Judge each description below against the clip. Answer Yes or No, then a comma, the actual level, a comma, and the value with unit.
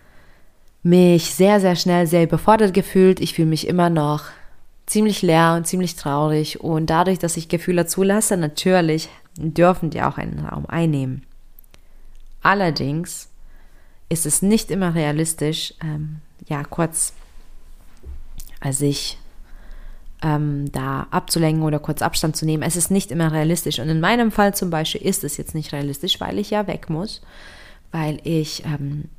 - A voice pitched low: No, medium, 160 Hz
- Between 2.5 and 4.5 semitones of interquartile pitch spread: Yes, average, 3.5 semitones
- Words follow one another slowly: No, average, 150 wpm